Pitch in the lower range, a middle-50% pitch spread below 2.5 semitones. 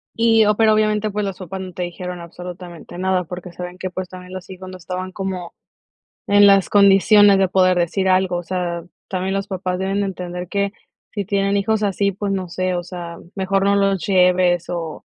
No: medium, 185 Hz; narrow, 1.8 semitones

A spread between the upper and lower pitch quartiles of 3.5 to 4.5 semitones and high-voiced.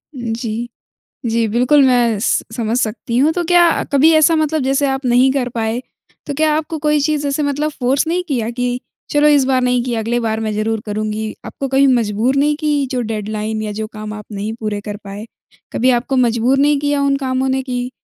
Yes: average, 4.2 semitones; very high, 250 Hz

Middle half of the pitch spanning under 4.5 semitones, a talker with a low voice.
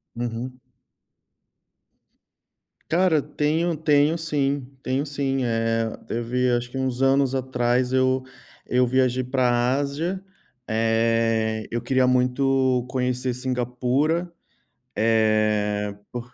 Yes: narrow, 2.6 semitones; low, 125 Hz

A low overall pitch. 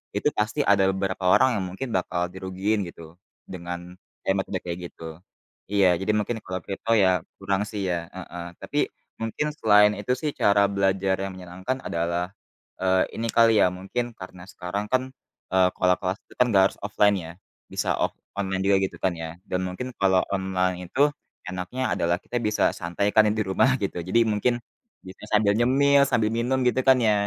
Yes: very low, 95 Hz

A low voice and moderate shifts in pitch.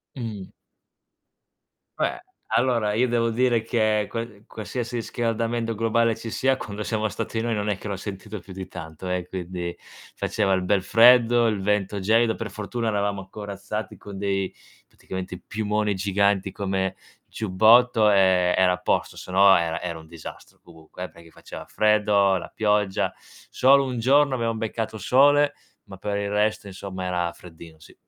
Yes: low, 105 Hz; average, 3.2 semitones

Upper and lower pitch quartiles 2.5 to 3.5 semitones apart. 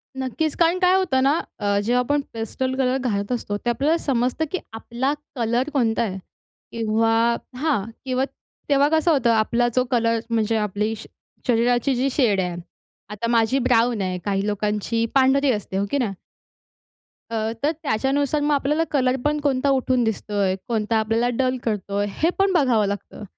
No: average, 3.9 semitones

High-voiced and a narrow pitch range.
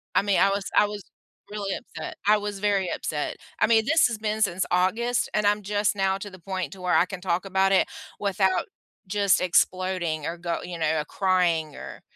Yes: high, 195 Hz; narrow, 2.2 semitones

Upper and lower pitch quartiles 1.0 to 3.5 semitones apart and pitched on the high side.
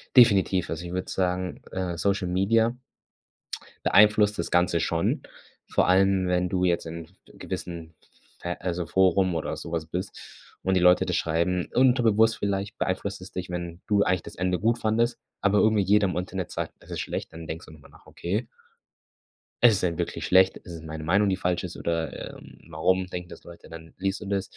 No: narrow, 2.6 semitones; very low, 90 Hz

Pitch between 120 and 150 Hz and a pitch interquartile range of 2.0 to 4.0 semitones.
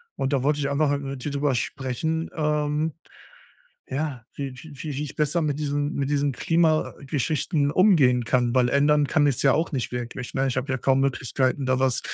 Yes: medium, 140 Hz; narrow, 2.4 semitones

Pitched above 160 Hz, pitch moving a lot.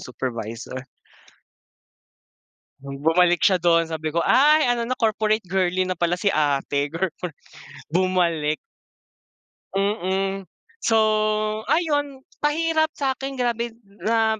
Yes: high, 190 Hz; wide, 5.9 semitones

